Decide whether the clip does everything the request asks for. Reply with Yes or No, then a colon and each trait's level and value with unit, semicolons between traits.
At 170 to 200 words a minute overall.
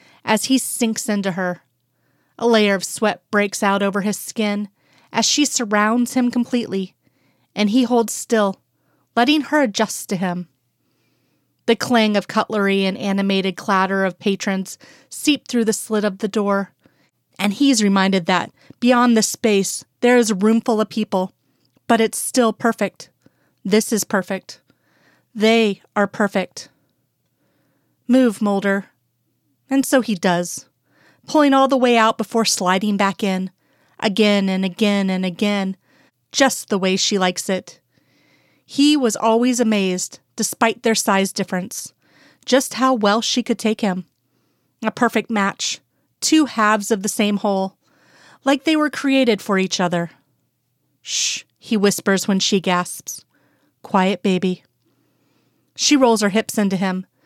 No: average, 145 wpm